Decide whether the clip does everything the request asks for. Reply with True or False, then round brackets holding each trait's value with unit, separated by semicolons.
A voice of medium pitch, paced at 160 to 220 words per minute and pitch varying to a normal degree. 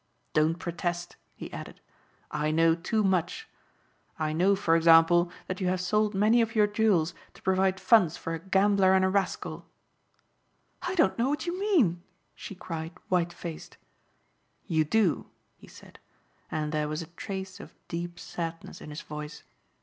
True (180 Hz; 165 wpm; 3.5 semitones)